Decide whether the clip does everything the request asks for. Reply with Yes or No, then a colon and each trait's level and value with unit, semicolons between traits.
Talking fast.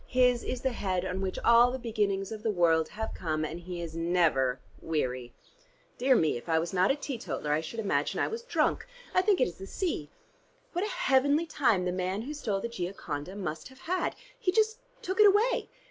Yes: fast, 215 wpm